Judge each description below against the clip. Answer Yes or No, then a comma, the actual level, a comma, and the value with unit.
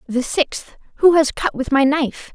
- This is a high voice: Yes, very high, 285 Hz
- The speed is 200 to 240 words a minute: Yes, fast, 205 wpm